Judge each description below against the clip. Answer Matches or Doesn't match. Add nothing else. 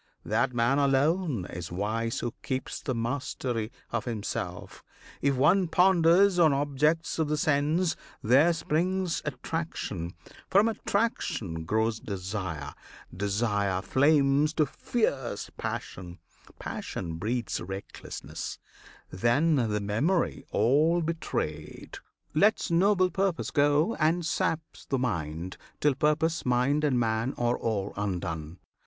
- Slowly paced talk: Matches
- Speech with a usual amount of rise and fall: Doesn't match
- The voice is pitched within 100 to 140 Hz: Matches